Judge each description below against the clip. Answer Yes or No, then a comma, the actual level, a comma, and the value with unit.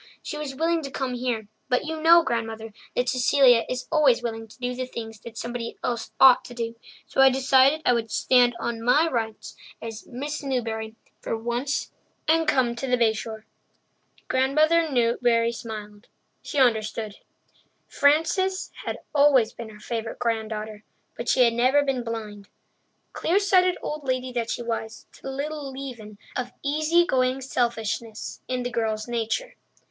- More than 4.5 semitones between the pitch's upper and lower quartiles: No, average, 3.4 semitones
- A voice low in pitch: No, high, 245 Hz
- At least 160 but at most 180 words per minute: Yes, average, 165 wpm